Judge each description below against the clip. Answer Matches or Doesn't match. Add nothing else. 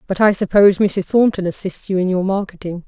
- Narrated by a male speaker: Doesn't match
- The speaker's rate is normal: Doesn't match